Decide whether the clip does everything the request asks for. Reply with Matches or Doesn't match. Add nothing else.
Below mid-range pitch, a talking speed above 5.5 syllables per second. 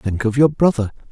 Doesn't match